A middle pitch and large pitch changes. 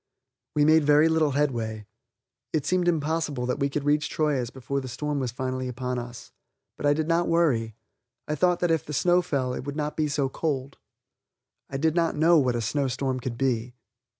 No: medium, 145 Hz; average, 3.6 semitones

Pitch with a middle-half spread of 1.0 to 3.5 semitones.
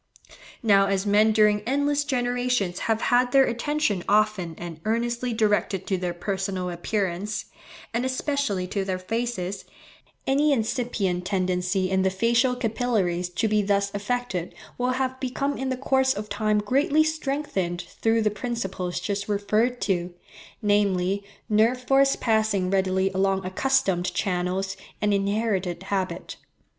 No: average, 4.5 semitones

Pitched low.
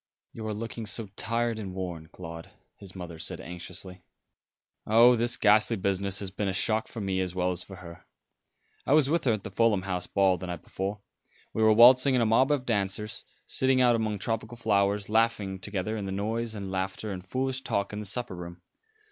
Yes: low, 105 Hz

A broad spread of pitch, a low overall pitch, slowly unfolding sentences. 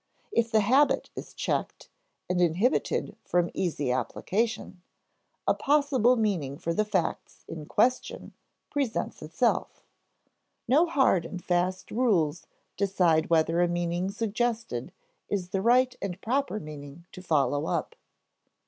No: wide, 5.7 semitones; medium, 185 Hz; slow, 125 wpm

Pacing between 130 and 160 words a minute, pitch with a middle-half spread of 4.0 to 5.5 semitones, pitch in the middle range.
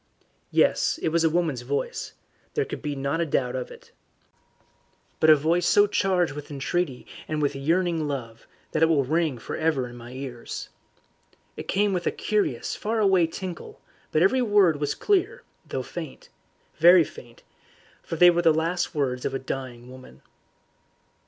No: average, 170 wpm; average, 4.6 semitones; medium, 160 Hz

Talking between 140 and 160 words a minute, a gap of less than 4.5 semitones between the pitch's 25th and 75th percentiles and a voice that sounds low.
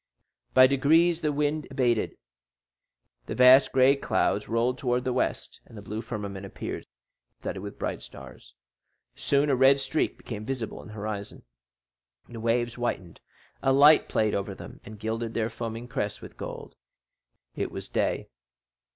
Yes: average, 150 wpm; average, 3.8 semitones; low, 120 Hz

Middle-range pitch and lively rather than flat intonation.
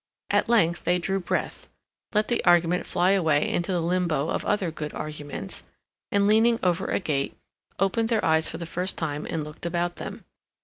No: medium, 175 Hz; average, 3.4 semitones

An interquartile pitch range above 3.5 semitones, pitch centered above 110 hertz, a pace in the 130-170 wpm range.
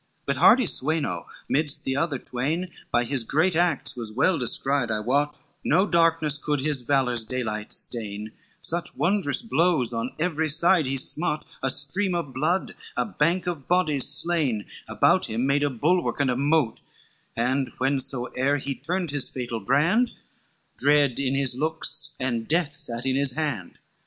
Yes: average, 4.2 semitones; medium, 140 Hz; average, 165 wpm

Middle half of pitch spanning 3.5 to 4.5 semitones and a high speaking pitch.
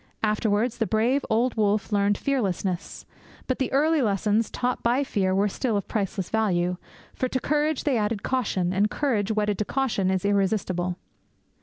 Yes: average, 4.2 semitones; high, 215 Hz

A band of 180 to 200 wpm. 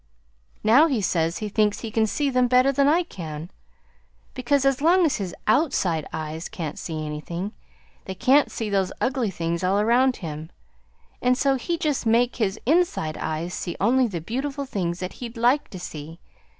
Yes: average, 185 wpm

